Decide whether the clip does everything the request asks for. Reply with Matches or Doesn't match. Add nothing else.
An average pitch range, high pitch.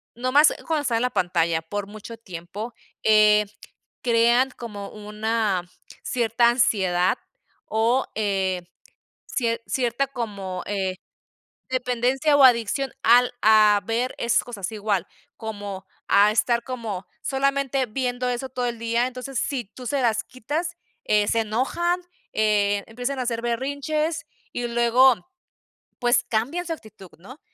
Matches